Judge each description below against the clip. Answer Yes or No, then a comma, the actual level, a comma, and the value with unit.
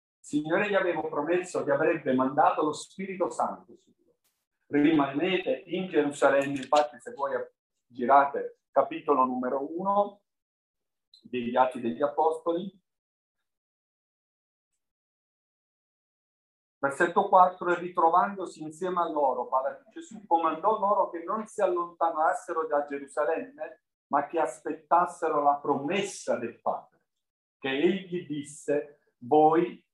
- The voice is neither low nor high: Yes, medium, 160 Hz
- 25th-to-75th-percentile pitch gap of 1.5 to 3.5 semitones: No, average, 3.9 semitones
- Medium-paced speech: No, slow, 105 wpm